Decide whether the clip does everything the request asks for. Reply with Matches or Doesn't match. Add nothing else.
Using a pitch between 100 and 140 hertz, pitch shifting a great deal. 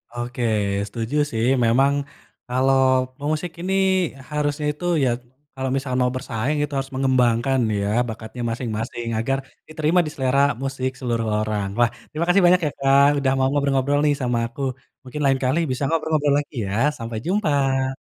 Doesn't match